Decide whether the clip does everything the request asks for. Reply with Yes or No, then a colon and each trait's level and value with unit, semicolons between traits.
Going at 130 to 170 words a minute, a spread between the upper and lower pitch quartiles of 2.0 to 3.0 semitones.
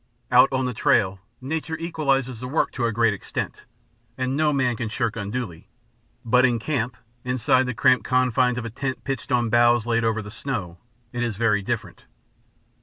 No: average, 185 wpm; narrow, 2.4 semitones